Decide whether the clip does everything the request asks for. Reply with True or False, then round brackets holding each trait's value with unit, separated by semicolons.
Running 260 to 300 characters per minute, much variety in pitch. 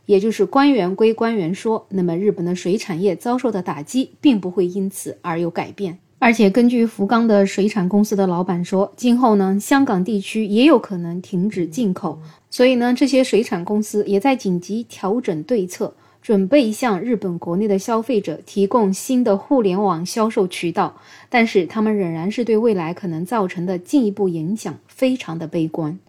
False (290 characters per minute; 3.9 semitones)